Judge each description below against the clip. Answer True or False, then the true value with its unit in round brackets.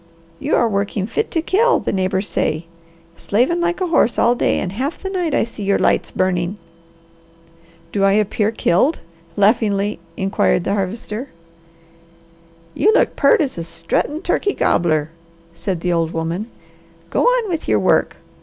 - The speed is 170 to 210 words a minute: False (160 wpm)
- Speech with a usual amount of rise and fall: False (7.9 semitones)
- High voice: True (210 Hz)